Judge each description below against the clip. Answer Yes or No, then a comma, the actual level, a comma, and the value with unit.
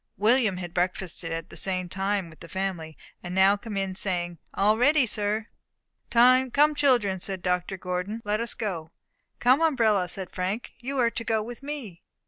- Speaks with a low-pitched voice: No, high, 200 Hz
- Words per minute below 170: No, average, 175 wpm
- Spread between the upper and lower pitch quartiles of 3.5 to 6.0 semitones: Yes, average, 4.3 semitones